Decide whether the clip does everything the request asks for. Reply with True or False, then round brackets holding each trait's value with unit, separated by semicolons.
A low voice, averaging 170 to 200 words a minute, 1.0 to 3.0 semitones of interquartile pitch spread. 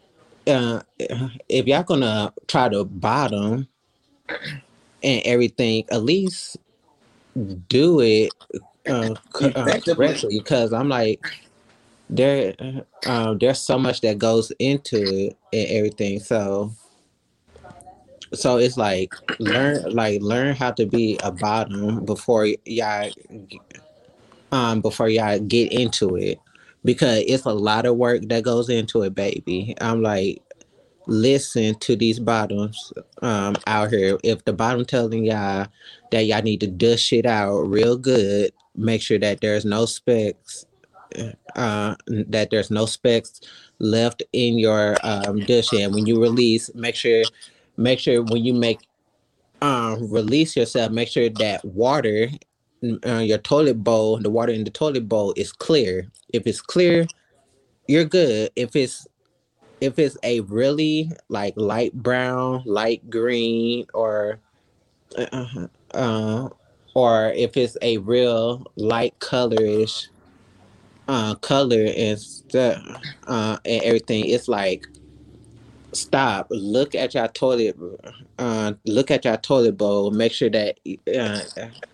False (115 Hz; 135 wpm; 2.6 semitones)